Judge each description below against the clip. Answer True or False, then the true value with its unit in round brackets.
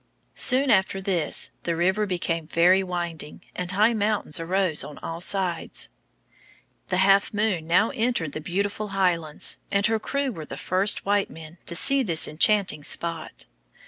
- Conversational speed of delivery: True (155 wpm)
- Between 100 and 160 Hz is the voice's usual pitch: False (185 Hz)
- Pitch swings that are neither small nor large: True (3.7 semitones)